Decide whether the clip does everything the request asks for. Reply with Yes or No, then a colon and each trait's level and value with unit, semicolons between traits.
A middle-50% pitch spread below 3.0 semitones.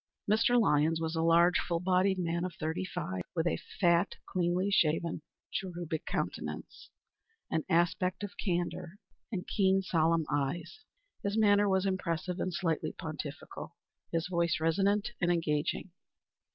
Yes: narrow, 2.6 semitones